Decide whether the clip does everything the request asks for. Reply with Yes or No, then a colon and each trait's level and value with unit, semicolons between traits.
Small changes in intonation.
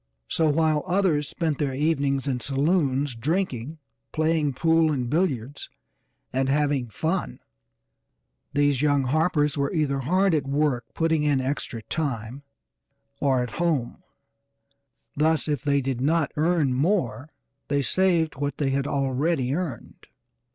No: average, 3.1 semitones